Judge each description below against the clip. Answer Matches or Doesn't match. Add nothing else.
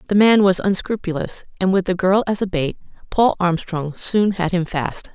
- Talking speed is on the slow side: Doesn't match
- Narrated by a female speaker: Matches